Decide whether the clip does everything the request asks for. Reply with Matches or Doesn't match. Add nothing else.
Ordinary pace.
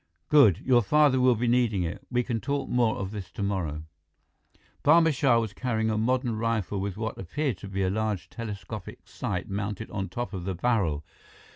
Matches